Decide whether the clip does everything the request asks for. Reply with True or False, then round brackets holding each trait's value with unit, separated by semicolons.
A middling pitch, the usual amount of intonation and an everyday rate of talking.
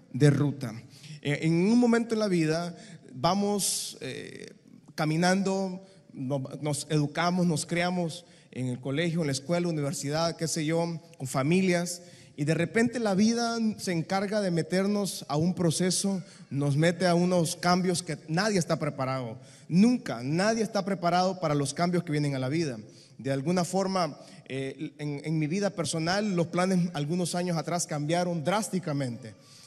True (170 Hz; 3.7 semitones; 155 wpm)